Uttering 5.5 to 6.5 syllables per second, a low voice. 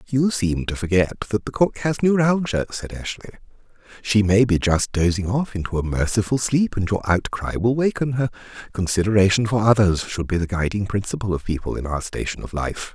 No: 5.3 syllables/s; low, 105 Hz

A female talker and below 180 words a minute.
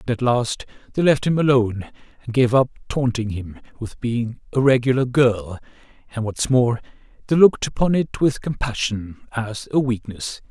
No: male; average, 165 wpm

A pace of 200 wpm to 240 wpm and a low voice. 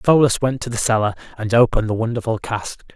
Yes: fast, 205 wpm; low, 115 Hz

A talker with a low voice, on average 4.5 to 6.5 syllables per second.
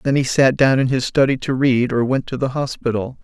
Yes: low, 130 Hz; 5.4 syllables/s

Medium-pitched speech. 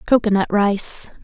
No: high, 210 Hz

